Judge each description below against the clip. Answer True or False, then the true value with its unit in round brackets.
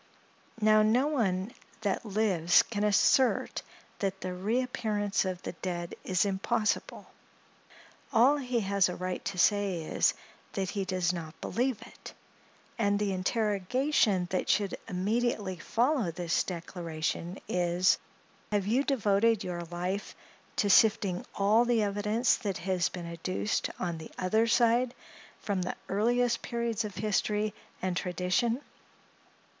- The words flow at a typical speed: False (130 wpm)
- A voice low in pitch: False (200 Hz)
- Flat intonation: False (3.7 semitones)